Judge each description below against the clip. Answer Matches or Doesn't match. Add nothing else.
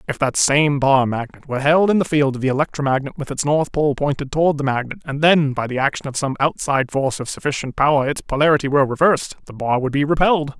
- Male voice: Matches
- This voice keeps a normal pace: Doesn't match